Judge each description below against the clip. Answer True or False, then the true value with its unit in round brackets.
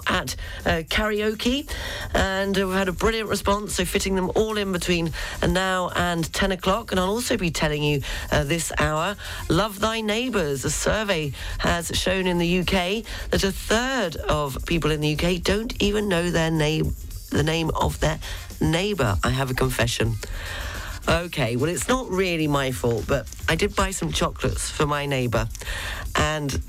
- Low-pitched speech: False (170 Hz)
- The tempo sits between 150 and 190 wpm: True (175 wpm)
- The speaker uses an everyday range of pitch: False (6.3 semitones)